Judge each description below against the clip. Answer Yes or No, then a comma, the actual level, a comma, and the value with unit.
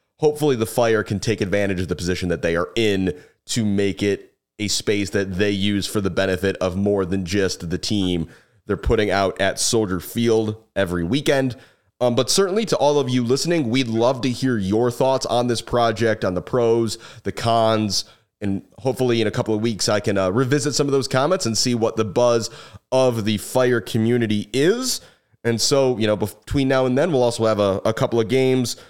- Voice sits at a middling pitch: No, low, 115 Hz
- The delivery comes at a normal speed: No, fast, 210 wpm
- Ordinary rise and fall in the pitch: Yes, average, 4.0 semitones